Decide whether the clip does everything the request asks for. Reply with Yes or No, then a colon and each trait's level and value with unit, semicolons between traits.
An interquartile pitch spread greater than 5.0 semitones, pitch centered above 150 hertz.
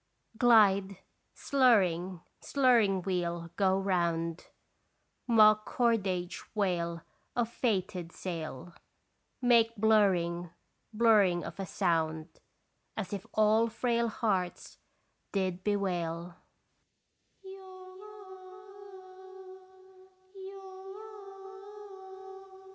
No: average, 4.0 semitones; high, 190 Hz